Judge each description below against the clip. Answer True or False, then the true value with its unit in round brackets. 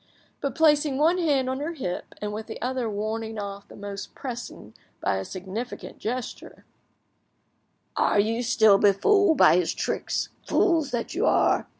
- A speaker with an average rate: True (160 wpm)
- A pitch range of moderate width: False (5.9 semitones)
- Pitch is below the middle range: False (235 Hz)